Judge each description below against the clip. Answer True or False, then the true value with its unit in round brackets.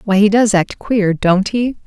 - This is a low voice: False (205 Hz)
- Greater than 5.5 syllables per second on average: False (4.2 syllables/s)